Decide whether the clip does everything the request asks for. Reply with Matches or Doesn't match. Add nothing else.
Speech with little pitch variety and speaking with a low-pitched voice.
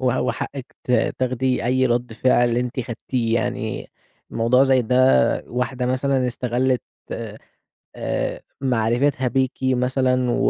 Matches